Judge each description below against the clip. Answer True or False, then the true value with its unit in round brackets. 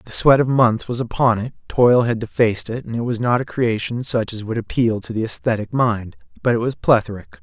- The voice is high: False (115 Hz)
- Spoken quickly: True (235 wpm)